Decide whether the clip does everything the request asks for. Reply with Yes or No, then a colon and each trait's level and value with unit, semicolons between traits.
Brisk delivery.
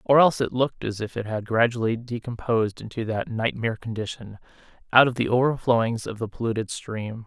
No: average, 180 wpm